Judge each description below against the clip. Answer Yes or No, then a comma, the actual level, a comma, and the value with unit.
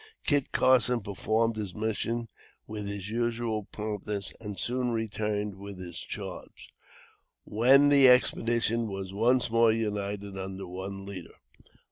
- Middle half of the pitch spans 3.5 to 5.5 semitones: No, average, 2.8 semitones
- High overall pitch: No, low, 105 Hz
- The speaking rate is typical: No, slow, 125 wpm